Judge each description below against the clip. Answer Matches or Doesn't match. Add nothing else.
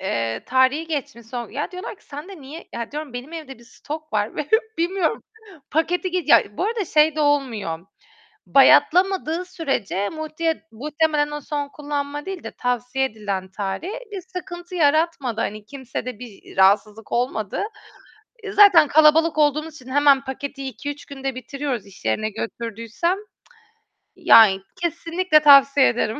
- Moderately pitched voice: Doesn't match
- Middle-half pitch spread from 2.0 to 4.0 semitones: Doesn't match